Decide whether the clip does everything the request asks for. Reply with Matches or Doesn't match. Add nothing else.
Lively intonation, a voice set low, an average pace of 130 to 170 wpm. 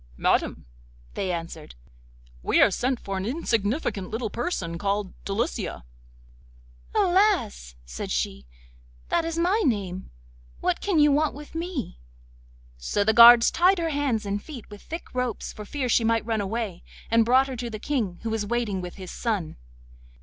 Doesn't match